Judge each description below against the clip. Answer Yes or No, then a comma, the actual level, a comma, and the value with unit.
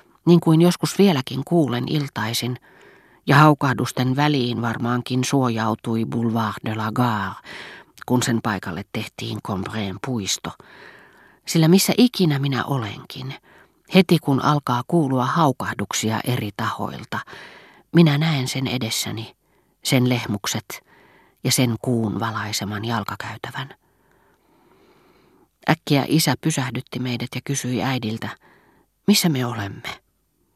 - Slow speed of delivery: No, average, 105 wpm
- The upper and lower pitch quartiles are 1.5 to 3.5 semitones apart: No, average, 4.2 semitones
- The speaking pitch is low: Yes, low, 125 Hz